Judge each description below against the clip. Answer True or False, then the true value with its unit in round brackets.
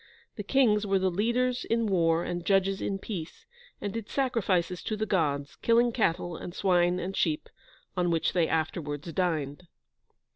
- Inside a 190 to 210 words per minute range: False (160 wpm)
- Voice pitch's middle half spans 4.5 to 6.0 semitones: False (4.1 semitones)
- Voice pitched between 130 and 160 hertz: False (185 Hz)